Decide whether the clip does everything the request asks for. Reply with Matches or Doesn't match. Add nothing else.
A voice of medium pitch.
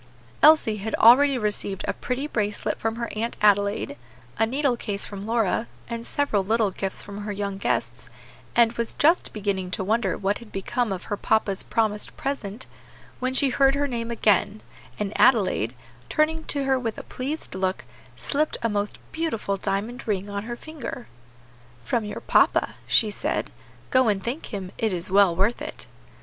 Doesn't match